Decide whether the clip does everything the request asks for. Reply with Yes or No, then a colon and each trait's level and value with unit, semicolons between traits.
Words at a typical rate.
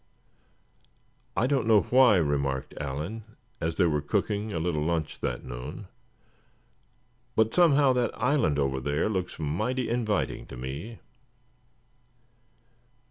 No: slow, 120 wpm